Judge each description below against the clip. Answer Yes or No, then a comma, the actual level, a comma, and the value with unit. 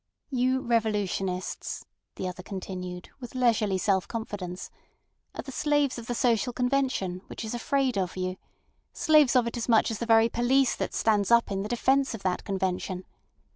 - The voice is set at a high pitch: Yes, high, 225 Hz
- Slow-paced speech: No, average, 175 wpm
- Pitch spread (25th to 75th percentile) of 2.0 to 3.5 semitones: No, average, 4.8 semitones